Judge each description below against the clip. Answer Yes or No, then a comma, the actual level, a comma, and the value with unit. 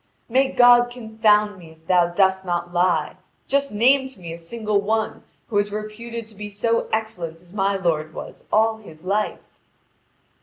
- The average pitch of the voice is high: Yes, high, 210 Hz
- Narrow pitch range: No, average, 4.1 semitones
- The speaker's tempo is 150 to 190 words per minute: Yes, average, 175 wpm